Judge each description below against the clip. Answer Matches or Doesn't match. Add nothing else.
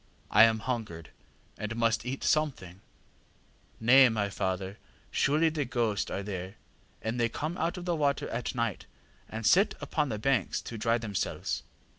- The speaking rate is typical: Matches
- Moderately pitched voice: Doesn't match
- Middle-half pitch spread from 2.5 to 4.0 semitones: Doesn't match